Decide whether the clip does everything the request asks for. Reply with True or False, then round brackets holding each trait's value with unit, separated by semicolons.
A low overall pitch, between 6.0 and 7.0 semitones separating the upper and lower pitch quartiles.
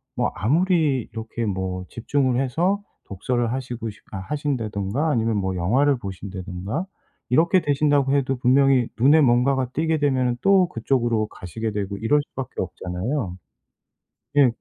False (125 Hz; 5.5 semitones)